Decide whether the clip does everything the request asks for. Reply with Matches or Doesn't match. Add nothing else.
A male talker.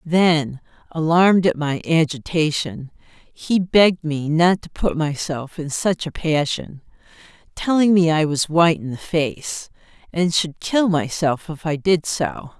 Doesn't match